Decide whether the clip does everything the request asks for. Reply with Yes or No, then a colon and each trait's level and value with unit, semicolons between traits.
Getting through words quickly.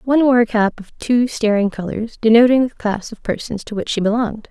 Yes: fast, 225 wpm